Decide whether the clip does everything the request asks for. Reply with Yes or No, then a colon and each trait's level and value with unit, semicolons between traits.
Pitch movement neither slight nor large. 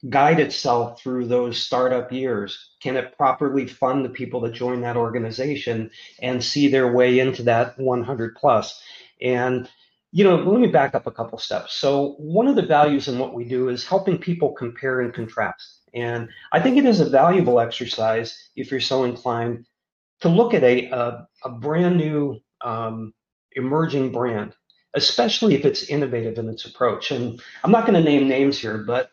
Yes: average, 3.1 semitones